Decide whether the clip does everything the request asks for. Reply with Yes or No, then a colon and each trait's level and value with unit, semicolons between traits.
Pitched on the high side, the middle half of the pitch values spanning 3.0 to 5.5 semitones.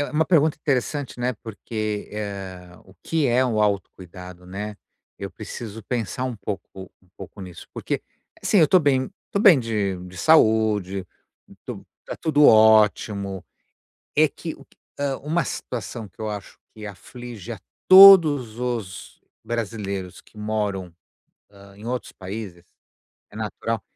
No: low, 110 Hz; average, 4.4 semitones